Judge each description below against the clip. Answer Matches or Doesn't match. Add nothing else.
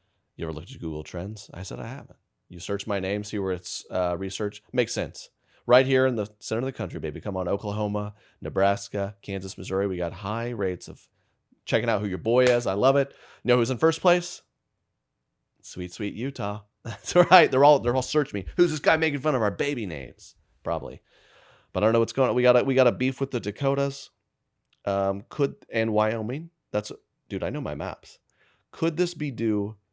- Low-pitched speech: Matches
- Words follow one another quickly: Matches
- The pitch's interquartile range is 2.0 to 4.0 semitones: Doesn't match